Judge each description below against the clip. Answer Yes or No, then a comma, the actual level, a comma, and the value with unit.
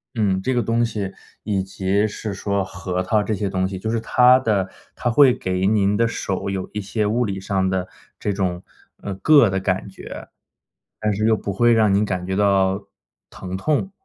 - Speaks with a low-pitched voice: Yes, low, 100 Hz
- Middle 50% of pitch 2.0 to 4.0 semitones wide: Yes, average, 2.7 semitones